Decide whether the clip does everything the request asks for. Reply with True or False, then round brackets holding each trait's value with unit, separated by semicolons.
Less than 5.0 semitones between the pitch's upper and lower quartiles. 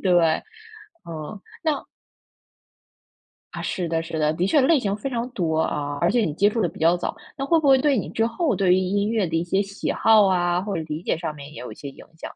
False (5.5 semitones)